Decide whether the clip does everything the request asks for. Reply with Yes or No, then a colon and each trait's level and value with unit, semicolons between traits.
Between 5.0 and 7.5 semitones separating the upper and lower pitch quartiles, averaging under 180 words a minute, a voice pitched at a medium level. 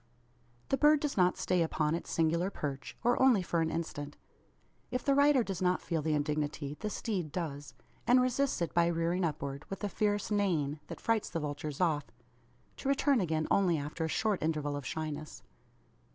No: wide, 5.4 semitones; average, 185 wpm; medium, 170 Hz